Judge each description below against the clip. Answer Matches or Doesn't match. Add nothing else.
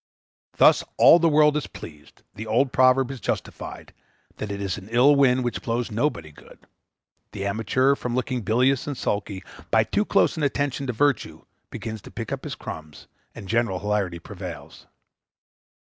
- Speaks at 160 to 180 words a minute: Matches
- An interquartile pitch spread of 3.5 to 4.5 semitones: Doesn't match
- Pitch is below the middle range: Matches